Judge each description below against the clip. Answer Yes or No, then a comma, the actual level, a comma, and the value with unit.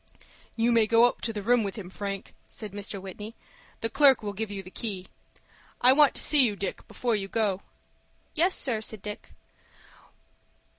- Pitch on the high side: Yes, high, 215 Hz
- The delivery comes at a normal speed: Yes, average, 185 wpm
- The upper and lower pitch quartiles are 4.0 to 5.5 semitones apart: No, average, 3.1 semitones